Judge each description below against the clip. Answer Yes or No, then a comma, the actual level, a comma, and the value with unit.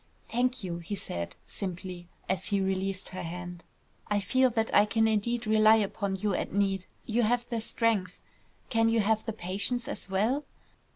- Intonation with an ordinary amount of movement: Yes, average, 3.1 semitones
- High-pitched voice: Yes, high, 205 Hz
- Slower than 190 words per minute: Yes, average, 175 wpm